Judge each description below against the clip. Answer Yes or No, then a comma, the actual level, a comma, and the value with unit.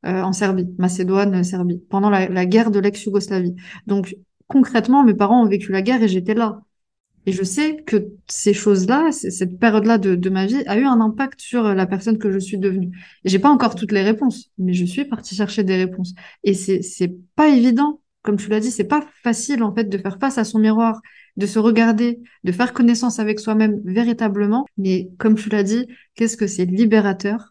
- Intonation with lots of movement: No, average, 3.3 semitones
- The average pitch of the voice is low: No, high, 210 Hz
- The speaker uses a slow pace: No, average, 215 wpm